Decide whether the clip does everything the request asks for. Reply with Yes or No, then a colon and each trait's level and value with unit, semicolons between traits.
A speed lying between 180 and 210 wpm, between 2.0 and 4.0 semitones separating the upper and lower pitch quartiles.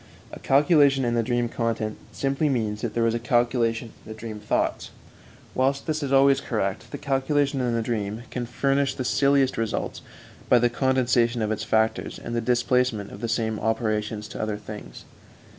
Yes: average, 185 wpm; average, 3.3 semitones